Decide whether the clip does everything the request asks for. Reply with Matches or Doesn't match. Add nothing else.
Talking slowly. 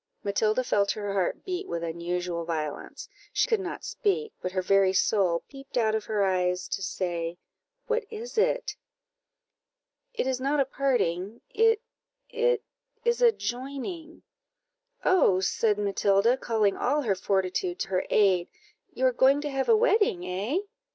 Doesn't match